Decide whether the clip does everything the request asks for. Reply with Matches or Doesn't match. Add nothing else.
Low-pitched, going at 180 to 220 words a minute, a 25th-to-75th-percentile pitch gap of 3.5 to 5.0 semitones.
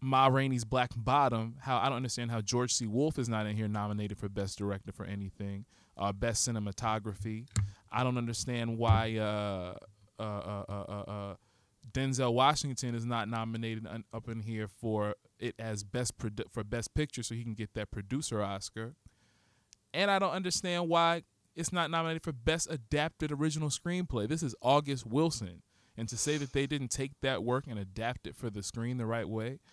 Matches